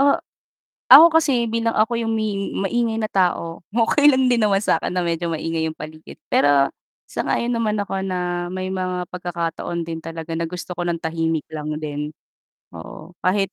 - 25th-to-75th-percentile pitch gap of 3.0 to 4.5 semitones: No, average, 4.9 semitones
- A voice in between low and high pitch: Yes, medium, 180 Hz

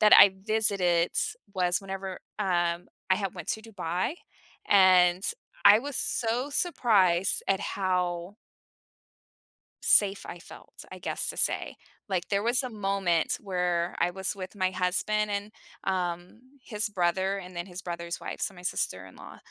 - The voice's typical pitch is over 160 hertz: Yes, high, 190 Hz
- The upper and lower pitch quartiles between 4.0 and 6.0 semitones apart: No, narrow, 2.5 semitones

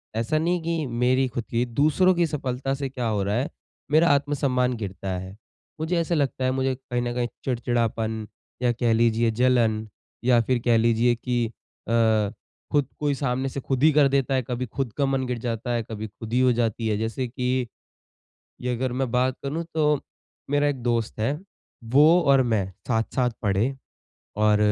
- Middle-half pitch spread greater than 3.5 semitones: No, average, 2.9 semitones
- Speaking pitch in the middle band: No, low, 125 Hz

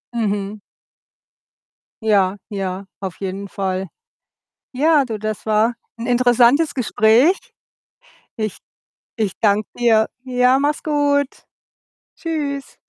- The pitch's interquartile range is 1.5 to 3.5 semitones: No, average, 4.9 semitones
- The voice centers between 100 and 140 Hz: No, high, 225 Hz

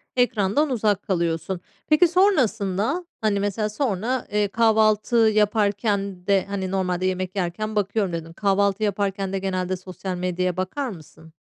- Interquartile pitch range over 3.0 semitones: No, average, 2.7 semitones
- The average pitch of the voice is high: Yes, high, 200 Hz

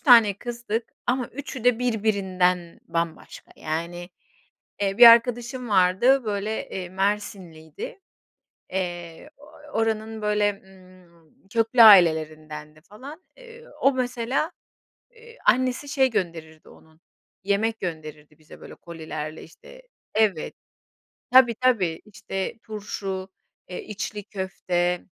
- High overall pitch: Yes, high, 200 Hz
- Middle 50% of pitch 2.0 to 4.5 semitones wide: No, average, 5.3 semitones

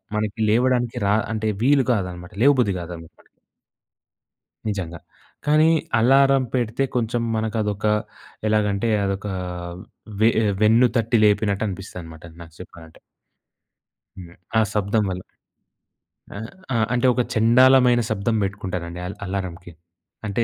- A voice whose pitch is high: No, low, 105 Hz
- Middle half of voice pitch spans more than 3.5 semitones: Yes, average, 4.1 semitones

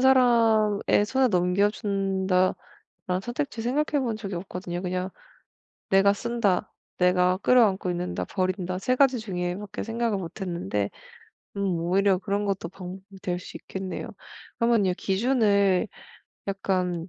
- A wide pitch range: No, average, 3.5 semitones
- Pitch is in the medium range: No, high, 195 Hz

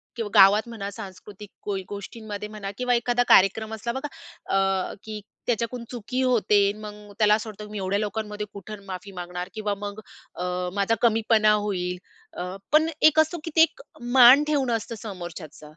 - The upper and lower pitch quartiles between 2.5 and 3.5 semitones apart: Yes, average, 2.9 semitones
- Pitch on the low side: No, high, 210 Hz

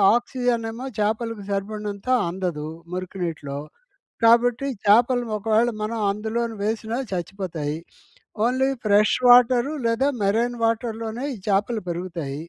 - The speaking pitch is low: No, high, 220 Hz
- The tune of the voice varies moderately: Yes, average, 3.3 semitones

